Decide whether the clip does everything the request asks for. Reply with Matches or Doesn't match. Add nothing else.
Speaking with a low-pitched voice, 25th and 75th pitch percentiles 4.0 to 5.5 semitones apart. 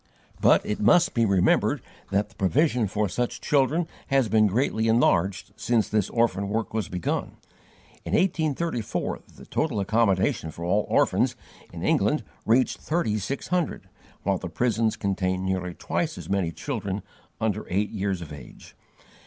Matches